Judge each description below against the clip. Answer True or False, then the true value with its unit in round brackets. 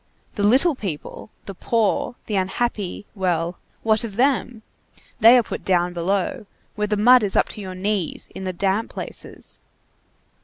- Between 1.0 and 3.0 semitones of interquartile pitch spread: False (3.4 semitones)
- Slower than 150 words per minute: False (160 wpm)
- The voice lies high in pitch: True (205 Hz)